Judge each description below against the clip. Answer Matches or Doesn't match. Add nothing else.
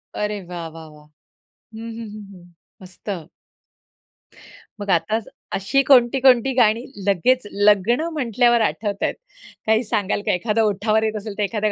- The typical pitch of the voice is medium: Doesn't match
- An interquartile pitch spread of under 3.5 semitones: Matches